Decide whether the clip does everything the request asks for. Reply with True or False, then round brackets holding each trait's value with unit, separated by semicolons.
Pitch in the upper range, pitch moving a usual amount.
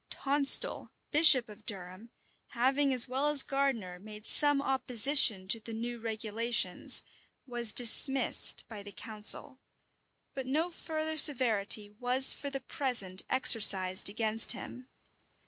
True (240 Hz; 4.3 semitones)